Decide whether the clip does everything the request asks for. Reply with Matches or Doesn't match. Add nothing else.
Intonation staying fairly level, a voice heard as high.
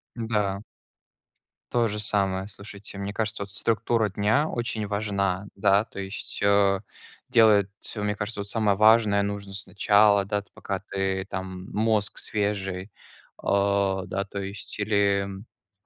Doesn't match